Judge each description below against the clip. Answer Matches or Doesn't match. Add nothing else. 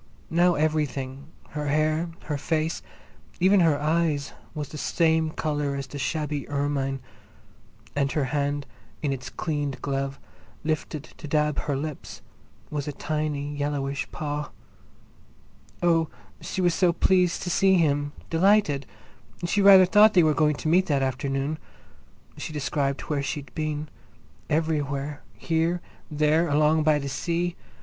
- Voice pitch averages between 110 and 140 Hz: Doesn't match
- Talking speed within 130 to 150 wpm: Matches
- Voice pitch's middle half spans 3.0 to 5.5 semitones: Doesn't match